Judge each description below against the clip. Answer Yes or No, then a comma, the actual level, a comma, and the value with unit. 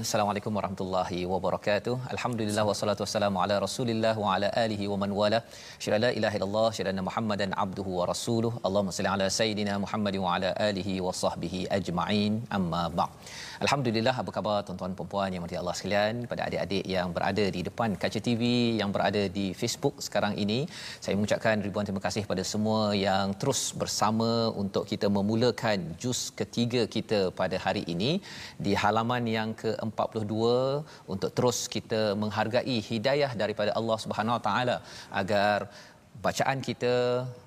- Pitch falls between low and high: No, low, 105 Hz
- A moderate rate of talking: No, fast, 150 wpm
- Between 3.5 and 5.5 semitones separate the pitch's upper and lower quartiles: No, narrow, 2.5 semitones